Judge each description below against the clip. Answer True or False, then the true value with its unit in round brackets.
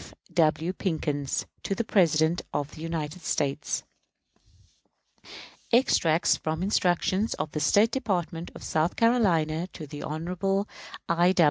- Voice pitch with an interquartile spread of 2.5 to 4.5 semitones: True (3.5 semitones)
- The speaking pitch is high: False (170 Hz)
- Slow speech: True (120 wpm)